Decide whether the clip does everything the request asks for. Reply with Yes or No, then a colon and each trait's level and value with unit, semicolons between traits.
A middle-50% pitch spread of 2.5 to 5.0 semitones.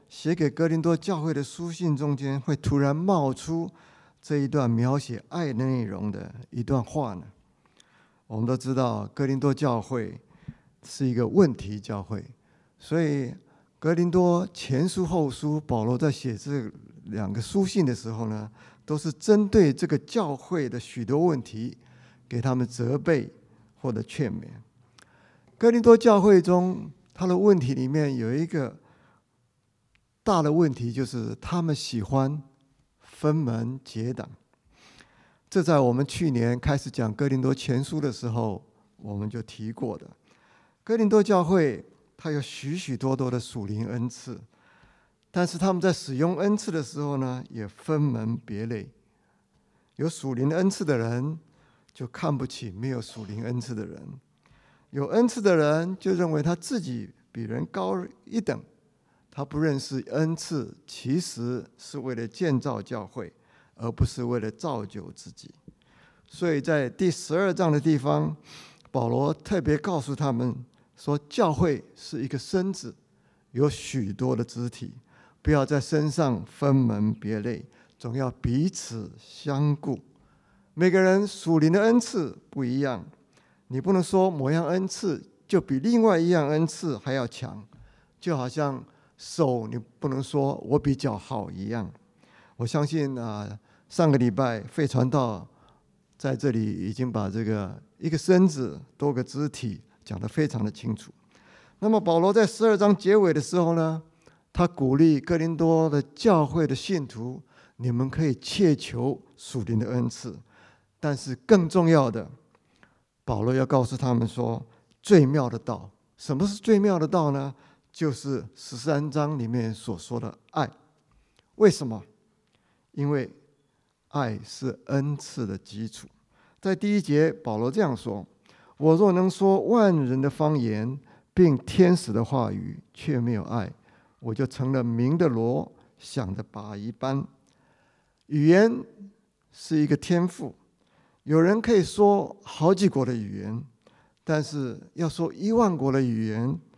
No: wide, 5.4 semitones